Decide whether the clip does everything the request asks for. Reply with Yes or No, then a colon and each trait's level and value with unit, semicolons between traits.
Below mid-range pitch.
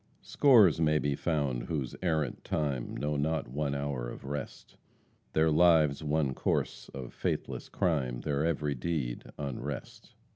Yes: very low, 75 Hz